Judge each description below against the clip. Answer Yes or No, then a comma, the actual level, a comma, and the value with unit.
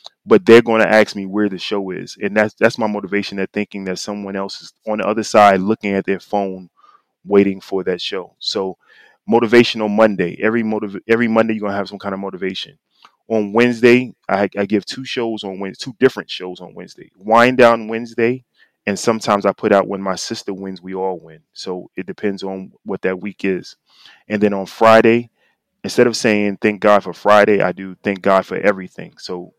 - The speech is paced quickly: Yes, fast, 210 wpm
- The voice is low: Yes, low, 105 Hz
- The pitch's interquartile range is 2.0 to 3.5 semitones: Yes, narrow, 2.6 semitones